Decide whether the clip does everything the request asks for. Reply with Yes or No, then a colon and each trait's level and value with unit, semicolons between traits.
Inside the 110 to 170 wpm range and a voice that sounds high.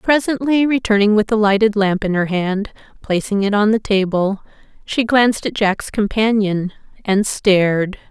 Yes: average, 150 wpm; high, 210 Hz